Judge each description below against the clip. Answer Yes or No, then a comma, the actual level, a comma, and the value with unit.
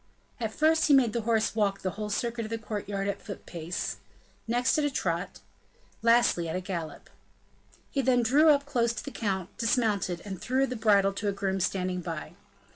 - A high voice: Yes, high, 215 Hz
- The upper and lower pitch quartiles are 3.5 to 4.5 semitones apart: Yes, average, 4.0 semitones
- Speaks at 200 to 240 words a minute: Yes, fast, 205 wpm